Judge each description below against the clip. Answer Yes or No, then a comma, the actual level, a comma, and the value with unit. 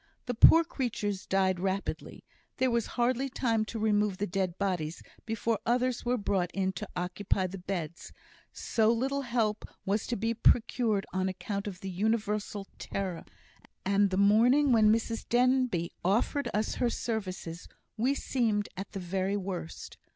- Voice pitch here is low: No, high, 210 Hz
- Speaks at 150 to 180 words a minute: Yes, average, 155 wpm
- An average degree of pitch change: Yes, average, 3.8 semitones